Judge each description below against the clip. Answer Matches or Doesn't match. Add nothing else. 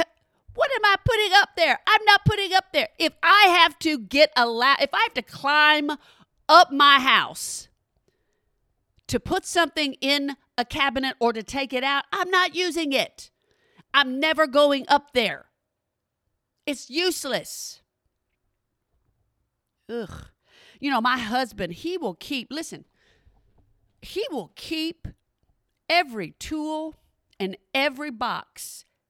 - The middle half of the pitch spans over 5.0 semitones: Doesn't match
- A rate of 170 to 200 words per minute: Doesn't match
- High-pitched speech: Matches